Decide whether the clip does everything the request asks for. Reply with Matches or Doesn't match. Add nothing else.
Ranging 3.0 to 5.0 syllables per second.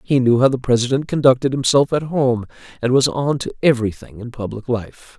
Doesn't match